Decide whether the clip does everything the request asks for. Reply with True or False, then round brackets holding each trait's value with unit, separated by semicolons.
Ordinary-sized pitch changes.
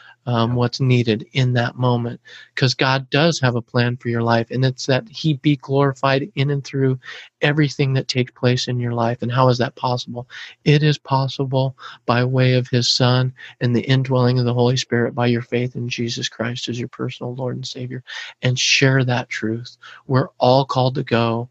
False (1.8 semitones)